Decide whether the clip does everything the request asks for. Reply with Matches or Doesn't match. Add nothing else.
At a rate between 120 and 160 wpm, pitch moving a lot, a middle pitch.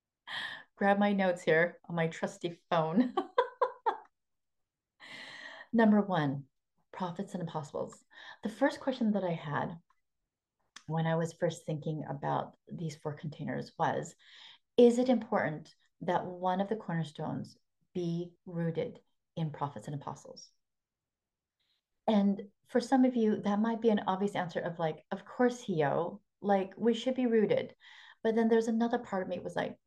Doesn't match